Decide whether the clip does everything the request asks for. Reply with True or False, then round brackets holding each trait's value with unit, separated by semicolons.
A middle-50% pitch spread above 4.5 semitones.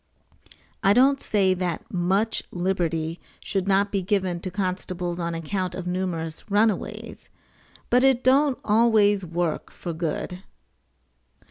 False (2.9 semitones)